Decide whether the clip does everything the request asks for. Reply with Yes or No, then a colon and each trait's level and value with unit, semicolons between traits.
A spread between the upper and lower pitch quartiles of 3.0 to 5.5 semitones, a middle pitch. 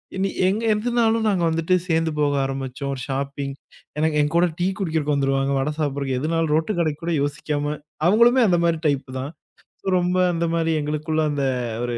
Yes: average, 3.7 semitones; medium, 155 Hz